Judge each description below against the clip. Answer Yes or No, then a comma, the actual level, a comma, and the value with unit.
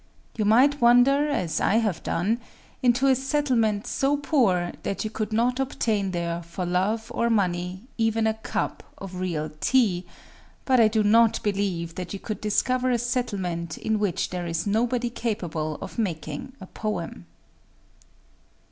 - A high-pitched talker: Yes, high, 215 Hz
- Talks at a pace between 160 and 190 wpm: No, average, 150 wpm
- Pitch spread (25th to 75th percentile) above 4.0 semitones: Yes, average, 5.0 semitones